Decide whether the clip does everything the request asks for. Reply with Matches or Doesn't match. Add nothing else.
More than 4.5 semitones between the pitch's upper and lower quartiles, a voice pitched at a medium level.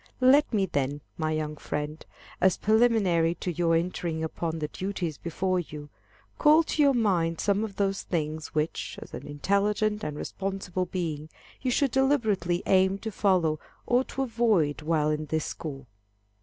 Matches